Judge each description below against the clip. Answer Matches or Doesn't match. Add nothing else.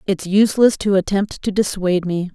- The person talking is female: Matches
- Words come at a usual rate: Matches